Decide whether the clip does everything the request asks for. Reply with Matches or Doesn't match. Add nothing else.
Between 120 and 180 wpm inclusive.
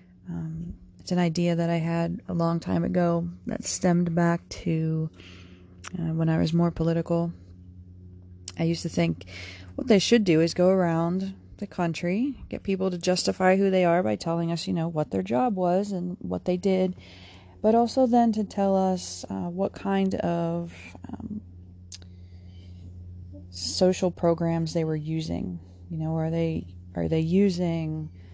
Matches